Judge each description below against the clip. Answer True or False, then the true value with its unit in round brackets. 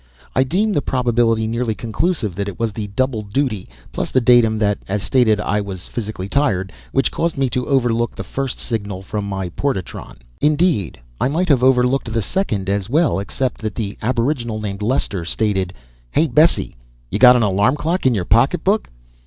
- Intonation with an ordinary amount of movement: True (4.6 semitones)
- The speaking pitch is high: False (115 Hz)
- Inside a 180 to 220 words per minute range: True (185 wpm)